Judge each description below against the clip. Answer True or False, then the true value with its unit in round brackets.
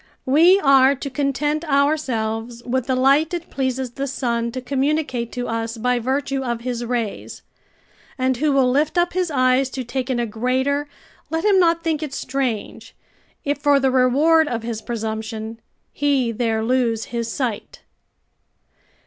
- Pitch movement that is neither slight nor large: True (3.2 semitones)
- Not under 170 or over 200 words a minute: False (160 wpm)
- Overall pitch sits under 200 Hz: False (260 Hz)